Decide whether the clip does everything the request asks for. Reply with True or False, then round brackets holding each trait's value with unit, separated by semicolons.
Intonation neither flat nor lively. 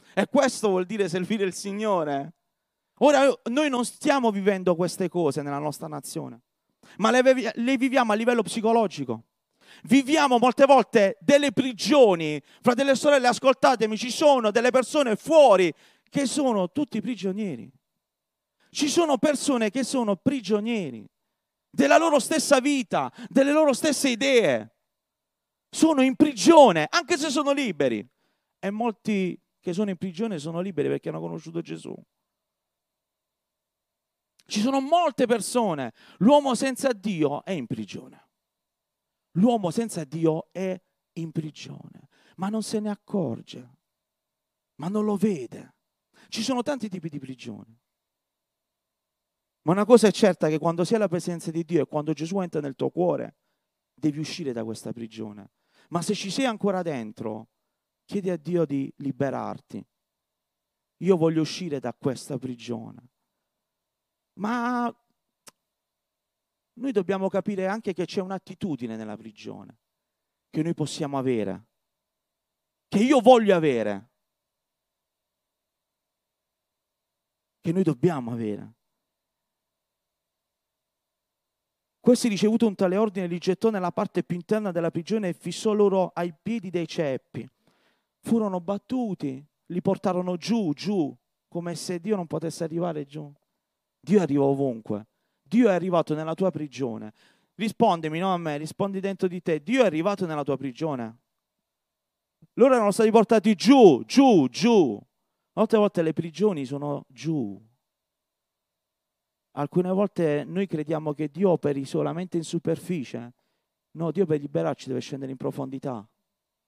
False (7.1 semitones)